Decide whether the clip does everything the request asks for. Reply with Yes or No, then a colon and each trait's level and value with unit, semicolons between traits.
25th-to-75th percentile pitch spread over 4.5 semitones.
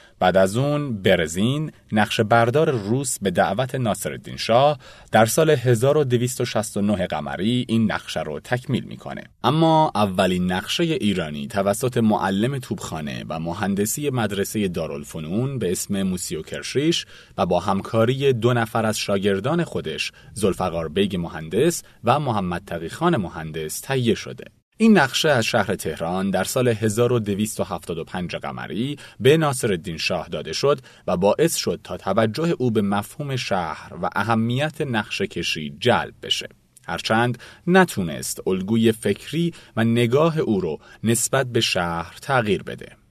Yes: average, 5.2 semitones